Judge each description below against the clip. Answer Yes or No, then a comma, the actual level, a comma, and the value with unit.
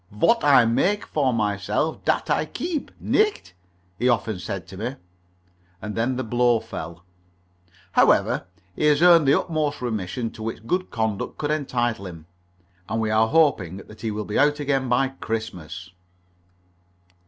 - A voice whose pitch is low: Yes, low, 115 Hz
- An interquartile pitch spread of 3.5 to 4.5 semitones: No, wide, 5.5 semitones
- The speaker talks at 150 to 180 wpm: Yes, average, 155 wpm